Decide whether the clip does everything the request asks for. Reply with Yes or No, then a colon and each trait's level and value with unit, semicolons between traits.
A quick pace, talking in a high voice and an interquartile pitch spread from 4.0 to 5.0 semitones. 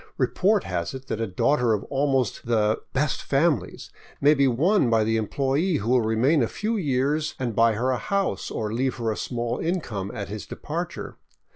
No: fast, 210 wpm; low, 125 Hz; average, 4.7 semitones